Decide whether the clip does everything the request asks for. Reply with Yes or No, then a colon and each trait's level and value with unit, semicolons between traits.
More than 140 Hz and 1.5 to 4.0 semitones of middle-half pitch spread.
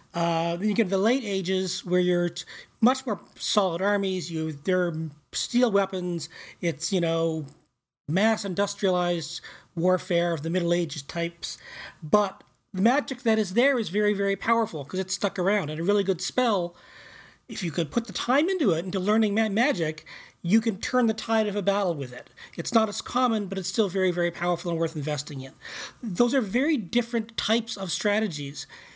No: high, 190 Hz; average, 4.6 semitones